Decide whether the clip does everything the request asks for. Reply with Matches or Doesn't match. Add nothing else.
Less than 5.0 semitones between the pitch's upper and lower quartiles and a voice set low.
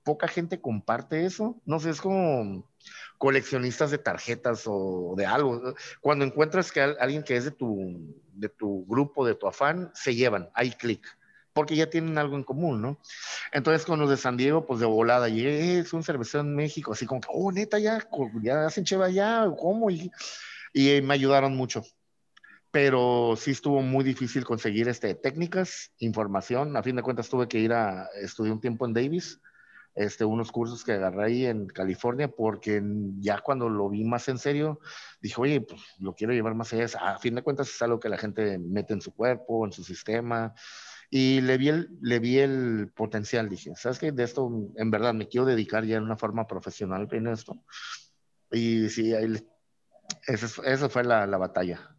Matches